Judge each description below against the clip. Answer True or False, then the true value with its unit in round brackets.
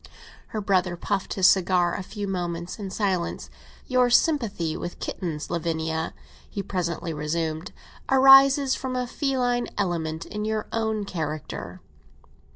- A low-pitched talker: False (190 Hz)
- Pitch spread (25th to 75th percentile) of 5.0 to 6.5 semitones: True (5.3 semitones)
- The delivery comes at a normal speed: False (130 wpm)